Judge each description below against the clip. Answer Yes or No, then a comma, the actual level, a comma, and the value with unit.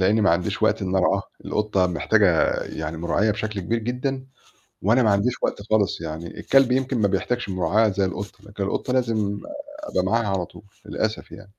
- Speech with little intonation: No, average, 3.5 semitones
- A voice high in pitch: No, low, 100 Hz